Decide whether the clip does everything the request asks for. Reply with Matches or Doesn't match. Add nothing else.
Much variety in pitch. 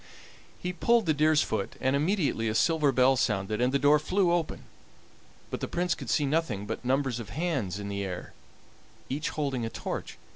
Matches